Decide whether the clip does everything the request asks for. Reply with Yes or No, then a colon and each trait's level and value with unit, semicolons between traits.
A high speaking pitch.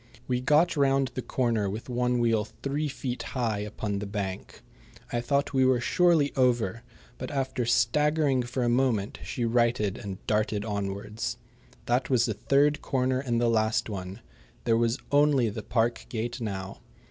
No: low, 120 Hz